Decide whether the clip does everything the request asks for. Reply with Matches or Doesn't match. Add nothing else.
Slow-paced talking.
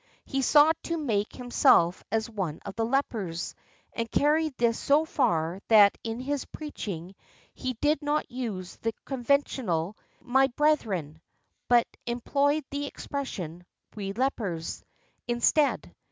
Matches